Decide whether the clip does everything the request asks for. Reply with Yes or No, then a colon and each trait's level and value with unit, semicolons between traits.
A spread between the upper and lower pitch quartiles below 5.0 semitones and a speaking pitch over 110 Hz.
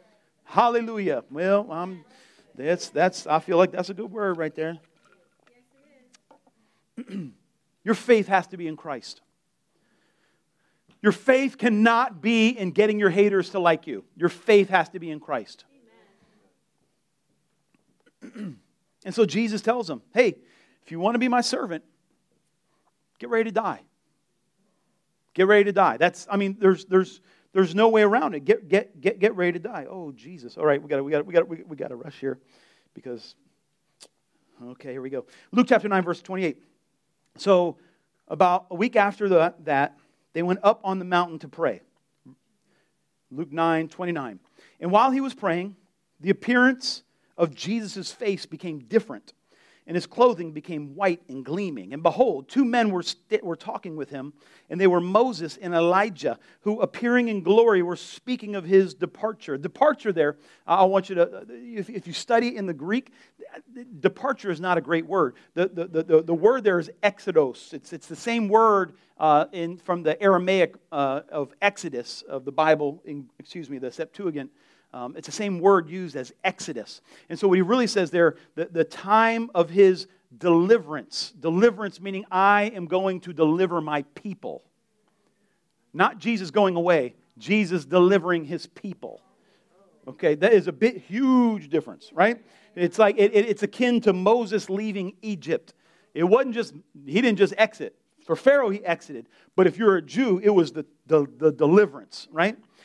Yes: average, 4.3 semitones; medium, 185 Hz